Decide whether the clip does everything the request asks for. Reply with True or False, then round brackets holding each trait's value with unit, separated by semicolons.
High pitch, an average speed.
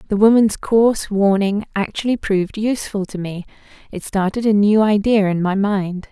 True (205 Hz; 165 wpm)